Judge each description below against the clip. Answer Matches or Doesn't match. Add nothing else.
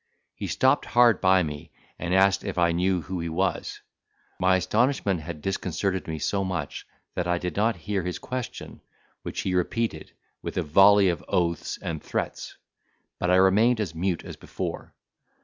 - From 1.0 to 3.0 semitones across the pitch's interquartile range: Matches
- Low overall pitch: Matches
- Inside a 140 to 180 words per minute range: Matches